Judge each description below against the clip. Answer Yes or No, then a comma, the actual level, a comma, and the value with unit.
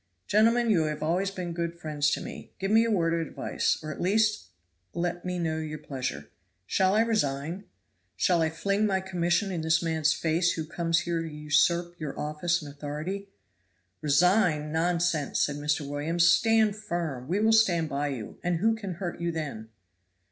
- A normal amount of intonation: Yes, average, 3.7 semitones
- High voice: No, medium, 170 Hz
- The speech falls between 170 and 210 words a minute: Yes, average, 185 wpm